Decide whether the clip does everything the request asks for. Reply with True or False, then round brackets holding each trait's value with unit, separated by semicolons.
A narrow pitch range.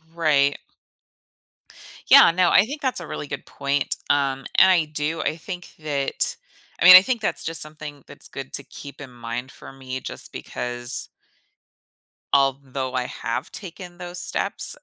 False (4.5 semitones)